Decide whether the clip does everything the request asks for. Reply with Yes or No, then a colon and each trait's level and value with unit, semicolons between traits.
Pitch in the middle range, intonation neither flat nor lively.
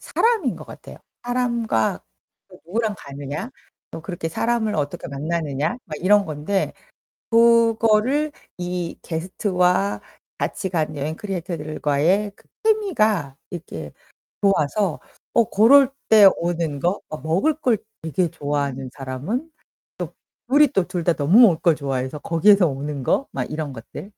No: medium, 175 Hz; wide, 6.6 semitones